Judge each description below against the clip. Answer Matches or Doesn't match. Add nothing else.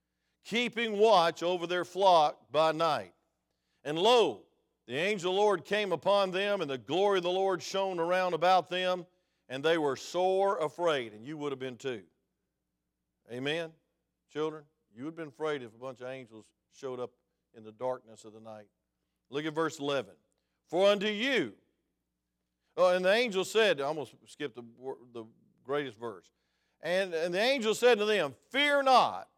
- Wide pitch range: Matches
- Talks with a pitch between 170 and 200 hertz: Doesn't match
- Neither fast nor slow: Matches